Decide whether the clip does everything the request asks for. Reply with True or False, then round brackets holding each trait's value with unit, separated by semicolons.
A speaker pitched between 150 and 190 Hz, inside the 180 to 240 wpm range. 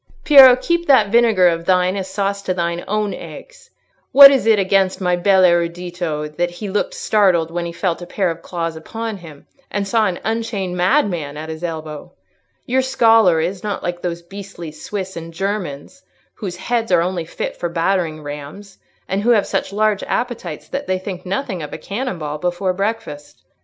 True (185 Hz; 190 wpm)